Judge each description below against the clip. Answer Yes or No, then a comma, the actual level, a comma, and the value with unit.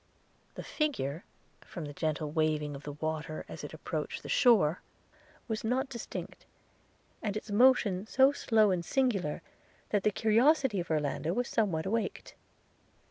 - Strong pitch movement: Yes, wide, 7.1 semitones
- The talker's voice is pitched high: Yes, high, 200 Hz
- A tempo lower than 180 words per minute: Yes, average, 150 wpm